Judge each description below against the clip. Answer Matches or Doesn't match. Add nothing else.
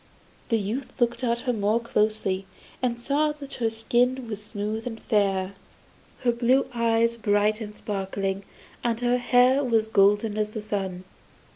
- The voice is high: Matches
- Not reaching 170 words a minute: Matches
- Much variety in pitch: Doesn't match